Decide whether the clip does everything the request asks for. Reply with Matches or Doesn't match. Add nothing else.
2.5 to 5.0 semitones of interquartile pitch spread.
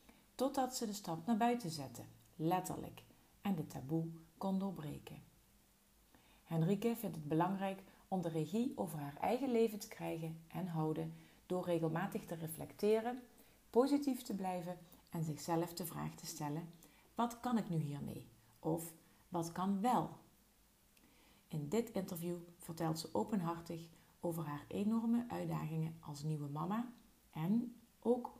Doesn't match